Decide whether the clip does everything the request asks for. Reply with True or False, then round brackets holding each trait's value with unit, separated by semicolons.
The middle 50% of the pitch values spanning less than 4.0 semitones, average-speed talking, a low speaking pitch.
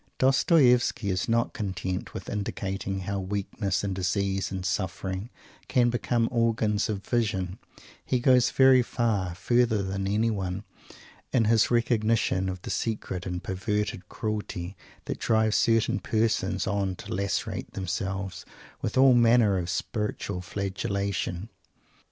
False (3.4 semitones; 125 wpm; 100 Hz)